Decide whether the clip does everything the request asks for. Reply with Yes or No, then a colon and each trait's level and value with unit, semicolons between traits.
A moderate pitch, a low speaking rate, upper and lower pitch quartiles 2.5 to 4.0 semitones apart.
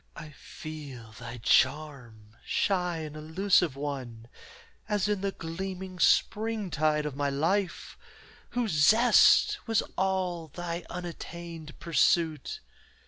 No: medium, 165 Hz; slow, 105 wpm; average, 4.5 semitones